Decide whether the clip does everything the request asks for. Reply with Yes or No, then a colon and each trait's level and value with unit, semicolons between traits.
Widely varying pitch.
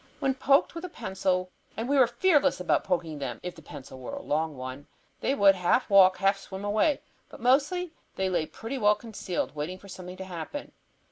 Yes: wide, 7.0 semitones